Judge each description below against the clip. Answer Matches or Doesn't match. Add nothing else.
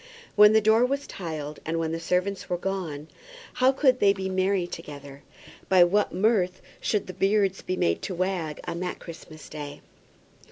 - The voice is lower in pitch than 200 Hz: Matches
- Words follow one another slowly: Doesn't match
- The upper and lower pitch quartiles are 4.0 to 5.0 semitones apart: Doesn't match